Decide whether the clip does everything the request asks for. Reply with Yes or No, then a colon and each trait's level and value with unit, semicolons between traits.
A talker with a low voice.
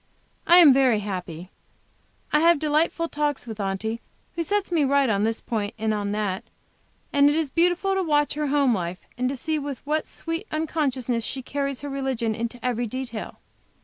No: very high, 270 Hz